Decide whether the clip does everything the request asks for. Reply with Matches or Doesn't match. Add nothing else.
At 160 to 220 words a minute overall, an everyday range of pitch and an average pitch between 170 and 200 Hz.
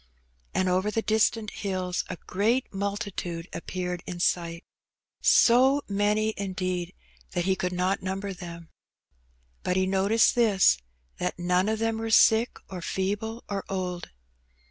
Doesn't match